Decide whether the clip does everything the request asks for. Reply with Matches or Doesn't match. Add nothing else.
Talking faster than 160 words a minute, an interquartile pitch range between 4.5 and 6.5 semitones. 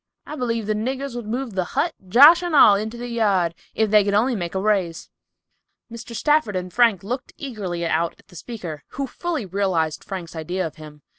Matches